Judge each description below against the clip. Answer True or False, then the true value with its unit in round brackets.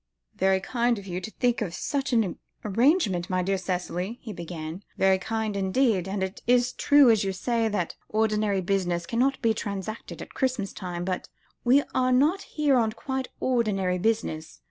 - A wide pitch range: False (4.6 semitones)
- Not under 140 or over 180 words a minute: True (175 wpm)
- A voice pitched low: False (210 Hz)